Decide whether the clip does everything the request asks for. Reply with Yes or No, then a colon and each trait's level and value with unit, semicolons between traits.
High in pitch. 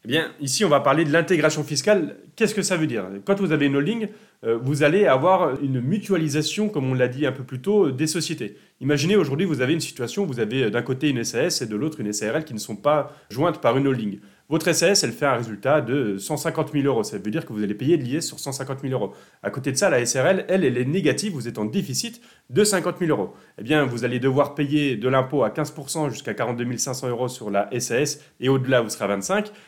No: medium, 145 Hz